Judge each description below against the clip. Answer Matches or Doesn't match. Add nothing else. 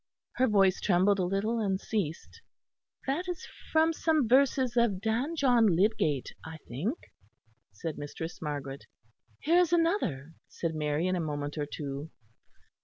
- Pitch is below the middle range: Doesn't match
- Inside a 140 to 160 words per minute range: Matches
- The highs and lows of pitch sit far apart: Matches